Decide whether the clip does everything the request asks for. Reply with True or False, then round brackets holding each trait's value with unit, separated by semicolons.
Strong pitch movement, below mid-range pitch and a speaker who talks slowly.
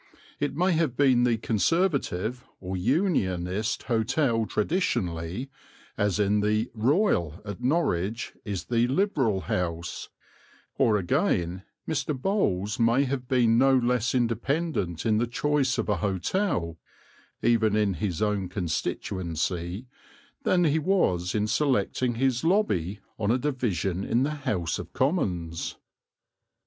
True (6.3 semitones; 115 Hz; 125 wpm)